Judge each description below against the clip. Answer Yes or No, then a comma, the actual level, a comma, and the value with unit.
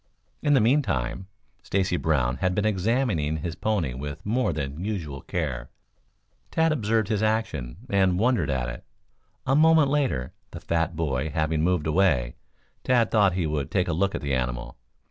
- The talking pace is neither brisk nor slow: Yes, average, 165 wpm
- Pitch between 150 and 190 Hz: No, very low, 90 Hz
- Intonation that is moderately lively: No, wide, 7.2 semitones